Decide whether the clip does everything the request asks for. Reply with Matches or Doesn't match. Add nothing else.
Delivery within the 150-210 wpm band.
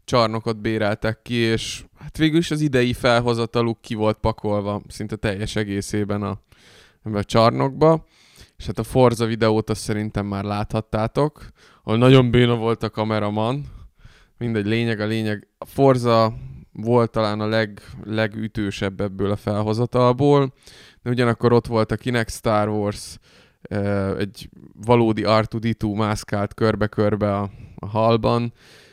Doesn't match